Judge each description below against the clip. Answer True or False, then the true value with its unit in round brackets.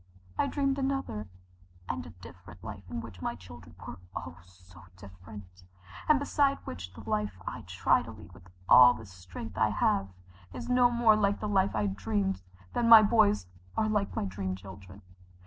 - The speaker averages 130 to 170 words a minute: False (180 wpm)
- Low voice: True (100 Hz)